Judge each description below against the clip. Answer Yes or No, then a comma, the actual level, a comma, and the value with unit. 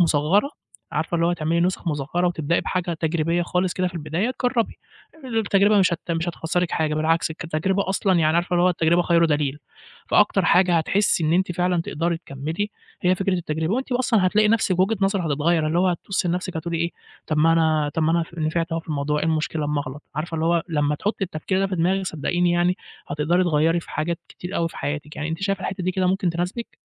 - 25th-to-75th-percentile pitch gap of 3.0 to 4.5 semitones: No, narrow, 2.6 semitones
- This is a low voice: No, medium, 170 Hz